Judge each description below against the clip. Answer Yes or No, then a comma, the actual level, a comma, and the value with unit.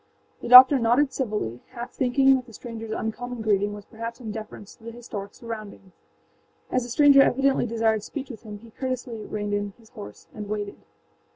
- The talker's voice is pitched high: Yes, high, 230 Hz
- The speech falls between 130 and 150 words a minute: No, average, 185 wpm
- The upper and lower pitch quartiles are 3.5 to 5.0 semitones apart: No, average, 3.0 semitones